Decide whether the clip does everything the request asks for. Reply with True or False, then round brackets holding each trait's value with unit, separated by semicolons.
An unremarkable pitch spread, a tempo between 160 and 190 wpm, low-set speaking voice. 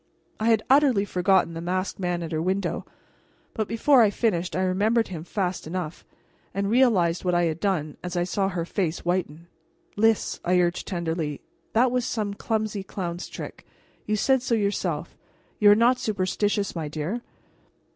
False (3.8 semitones; 175 wpm; 190 Hz)